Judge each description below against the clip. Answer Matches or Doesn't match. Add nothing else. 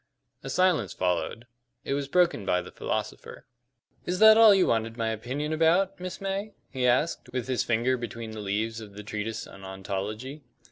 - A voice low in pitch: Matches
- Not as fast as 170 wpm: Doesn't match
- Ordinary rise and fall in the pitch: Doesn't match